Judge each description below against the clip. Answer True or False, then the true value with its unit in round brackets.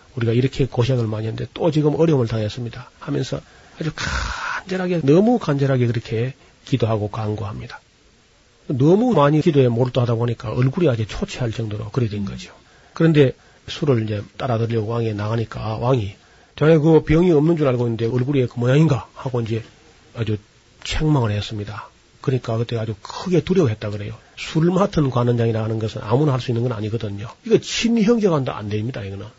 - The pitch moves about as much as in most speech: True (4.9 semitones)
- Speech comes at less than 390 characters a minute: False (400 characters per minute)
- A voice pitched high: False (120 Hz)